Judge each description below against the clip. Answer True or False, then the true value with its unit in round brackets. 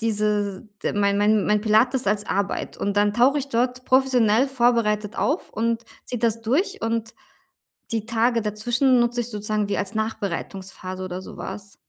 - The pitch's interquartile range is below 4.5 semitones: True (2.7 semitones)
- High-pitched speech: True (220 Hz)